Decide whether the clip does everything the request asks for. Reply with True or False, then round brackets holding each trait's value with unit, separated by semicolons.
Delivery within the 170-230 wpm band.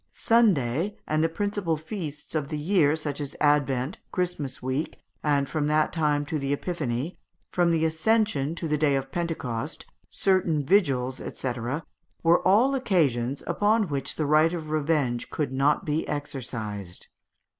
False (150 wpm)